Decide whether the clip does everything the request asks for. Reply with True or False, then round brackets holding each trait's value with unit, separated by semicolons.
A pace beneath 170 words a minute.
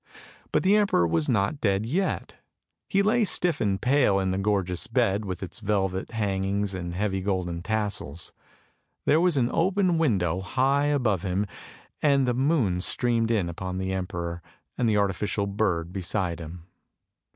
True (160 wpm)